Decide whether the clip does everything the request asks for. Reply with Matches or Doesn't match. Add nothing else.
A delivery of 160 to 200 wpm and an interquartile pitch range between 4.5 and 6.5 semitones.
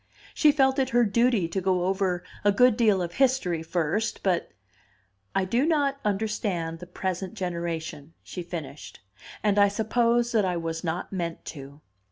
Matches